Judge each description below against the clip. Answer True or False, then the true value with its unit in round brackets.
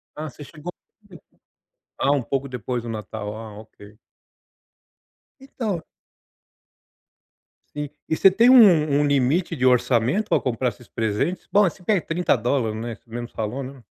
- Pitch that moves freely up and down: True (6.4 semitones)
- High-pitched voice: False (135 Hz)